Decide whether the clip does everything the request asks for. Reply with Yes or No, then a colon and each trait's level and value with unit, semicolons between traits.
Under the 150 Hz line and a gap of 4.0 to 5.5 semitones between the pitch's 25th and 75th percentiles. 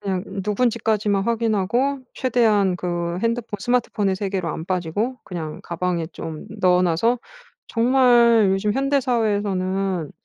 No: high, 205 Hz; average, 4.4 semitones